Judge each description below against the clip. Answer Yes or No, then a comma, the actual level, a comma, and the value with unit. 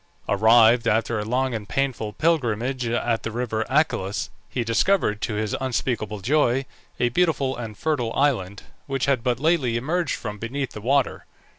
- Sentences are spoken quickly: No, average, 160 wpm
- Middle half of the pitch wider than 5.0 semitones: No, average, 3.6 semitones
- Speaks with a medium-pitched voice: No, low, 120 Hz